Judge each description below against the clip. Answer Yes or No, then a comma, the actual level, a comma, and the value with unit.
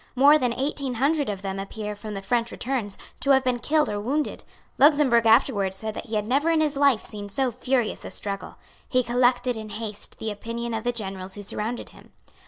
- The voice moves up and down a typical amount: Yes, average, 4.2 semitones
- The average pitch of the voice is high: Yes, high, 235 Hz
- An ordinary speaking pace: No, fast, 210 wpm